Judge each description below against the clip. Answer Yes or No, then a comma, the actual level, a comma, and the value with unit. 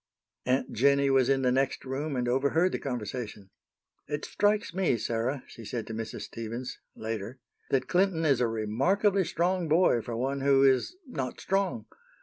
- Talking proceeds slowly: No, average, 165 wpm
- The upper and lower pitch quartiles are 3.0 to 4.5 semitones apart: No, average, 5.2 semitones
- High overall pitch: No, low, 135 Hz